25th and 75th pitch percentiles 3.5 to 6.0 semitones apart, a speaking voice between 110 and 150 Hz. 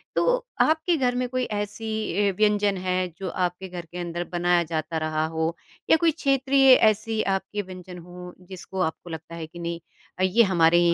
No: average, 4.1 semitones; medium, 185 Hz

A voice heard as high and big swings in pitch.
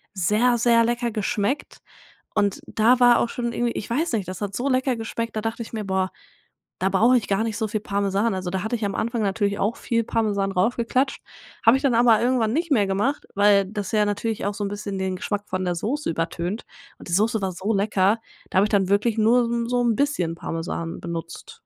No: high, 215 Hz; average, 3.2 semitones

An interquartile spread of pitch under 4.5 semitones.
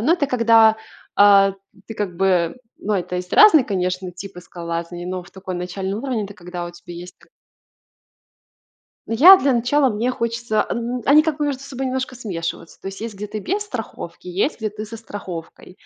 No: wide, 5.6 semitones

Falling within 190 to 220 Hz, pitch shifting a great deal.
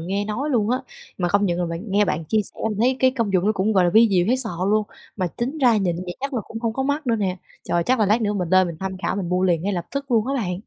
No: high, 205 Hz; average, 4.5 semitones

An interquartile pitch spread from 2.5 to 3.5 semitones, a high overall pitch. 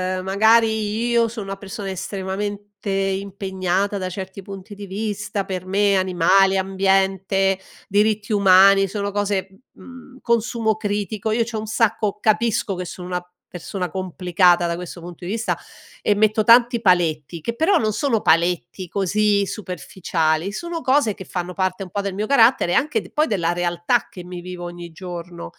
Yes: average, 2.9 semitones; high, 195 Hz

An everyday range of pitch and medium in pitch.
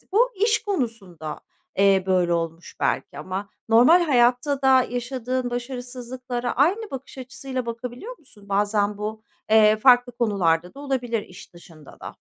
No: average, 4.6 semitones; high, 240 Hz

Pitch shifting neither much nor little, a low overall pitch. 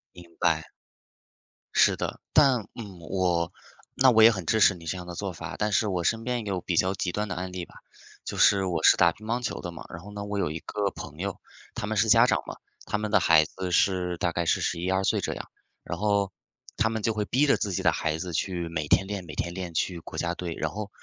Yes: average, 3.2 semitones; very low, 95 Hz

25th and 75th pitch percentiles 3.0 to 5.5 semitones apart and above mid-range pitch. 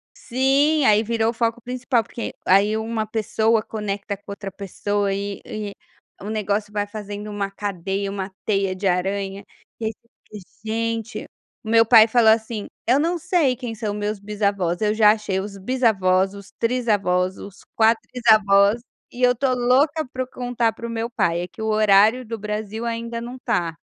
No: narrow, 2.6 semitones; high, 215 Hz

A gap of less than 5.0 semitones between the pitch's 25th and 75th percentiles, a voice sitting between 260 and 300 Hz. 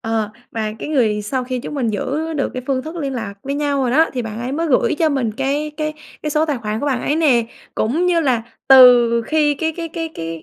Yes: average, 4.5 semitones; very high, 270 Hz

